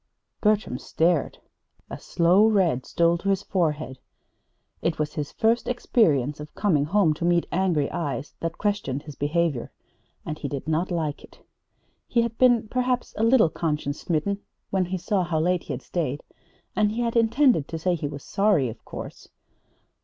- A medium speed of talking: Yes, average, 175 wpm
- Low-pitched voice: No, medium, 170 Hz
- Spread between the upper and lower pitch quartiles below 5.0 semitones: No, wide, 5.6 semitones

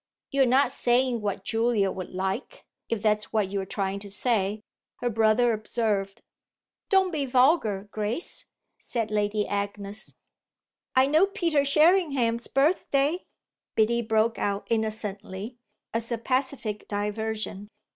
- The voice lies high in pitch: Yes, high, 225 Hz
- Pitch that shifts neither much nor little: Yes, average, 4.1 semitones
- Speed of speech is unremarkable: No, slow, 125 wpm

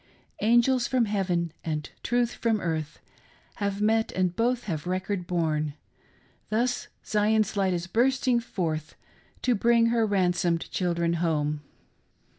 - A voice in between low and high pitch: No, high, 195 Hz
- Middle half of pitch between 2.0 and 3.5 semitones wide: No, average, 5.3 semitones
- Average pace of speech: No, slow, 125 wpm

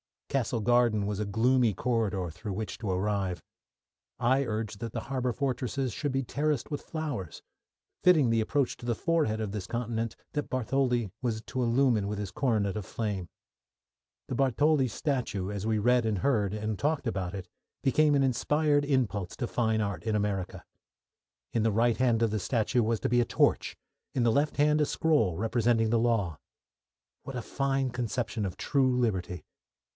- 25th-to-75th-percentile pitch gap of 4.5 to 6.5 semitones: No, average, 4.0 semitones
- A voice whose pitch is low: Yes, low, 115 Hz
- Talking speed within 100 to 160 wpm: No, average, 180 wpm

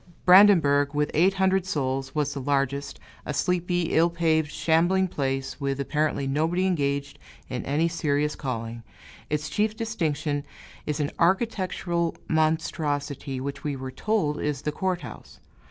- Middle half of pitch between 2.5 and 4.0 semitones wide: Yes, average, 3.7 semitones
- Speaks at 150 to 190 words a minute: No, average, 140 wpm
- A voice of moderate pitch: Yes, medium, 150 Hz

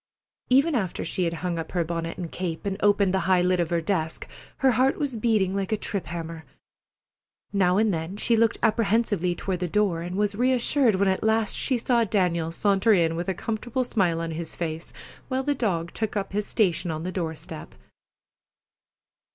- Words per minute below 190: No, average, 200 wpm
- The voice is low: No, high, 190 Hz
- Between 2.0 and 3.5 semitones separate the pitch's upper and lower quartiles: No, average, 4.5 semitones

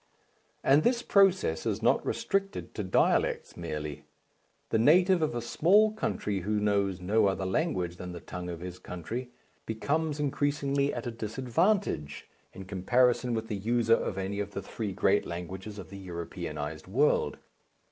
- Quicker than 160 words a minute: No, average, 155 wpm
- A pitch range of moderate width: No, wide, 7.6 semitones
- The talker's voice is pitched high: No, low, 105 Hz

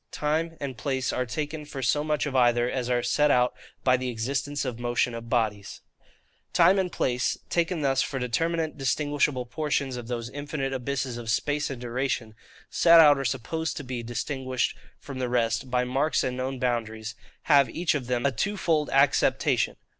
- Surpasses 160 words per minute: Yes, average, 180 wpm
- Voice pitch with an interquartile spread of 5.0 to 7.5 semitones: No, average, 3.2 semitones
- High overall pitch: No, low, 130 Hz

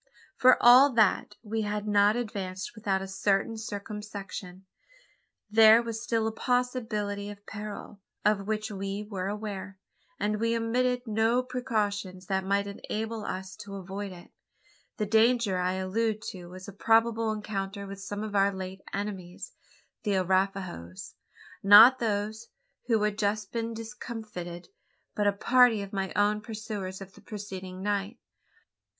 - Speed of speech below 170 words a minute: Yes, average, 145 wpm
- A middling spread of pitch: No, narrow, 2.3 semitones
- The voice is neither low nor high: No, high, 205 Hz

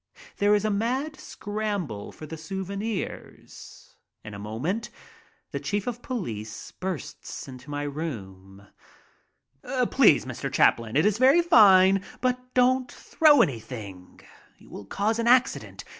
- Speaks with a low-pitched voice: No, high, 195 Hz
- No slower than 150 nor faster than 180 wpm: No, slow, 135 wpm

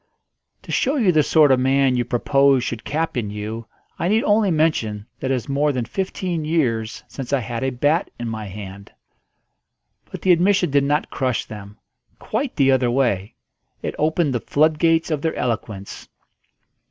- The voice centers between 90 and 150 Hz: Yes, low, 135 Hz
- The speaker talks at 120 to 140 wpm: No, average, 175 wpm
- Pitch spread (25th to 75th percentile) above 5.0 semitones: Yes, wide, 5.6 semitones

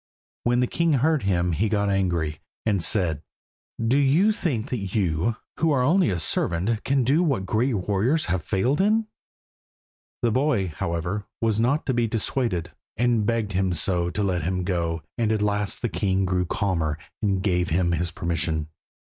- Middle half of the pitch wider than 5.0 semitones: Yes, wide, 5.5 semitones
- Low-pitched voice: Yes, low, 100 Hz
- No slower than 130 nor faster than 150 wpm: No, average, 175 wpm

